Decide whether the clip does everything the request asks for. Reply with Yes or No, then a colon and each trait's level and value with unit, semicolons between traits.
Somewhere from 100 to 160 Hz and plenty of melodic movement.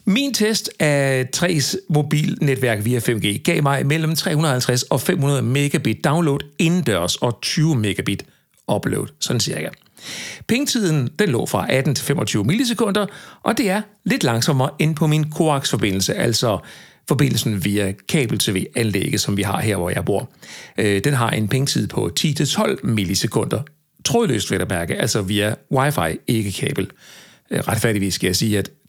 Yes: medium, 140 Hz; wide, 6.1 semitones